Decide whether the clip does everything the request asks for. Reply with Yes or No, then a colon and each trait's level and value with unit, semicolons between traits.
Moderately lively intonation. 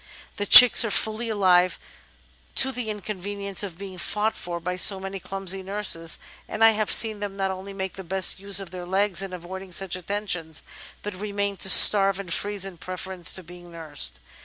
No: narrow, 2.1 semitones